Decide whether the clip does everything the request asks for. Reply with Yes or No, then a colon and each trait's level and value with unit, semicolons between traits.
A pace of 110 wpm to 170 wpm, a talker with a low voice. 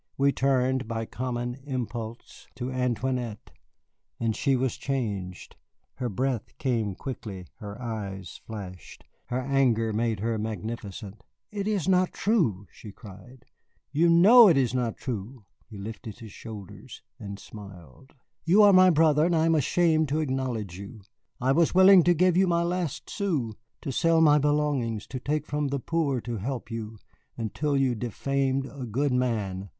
Yes: average, 155 wpm; low, 125 Hz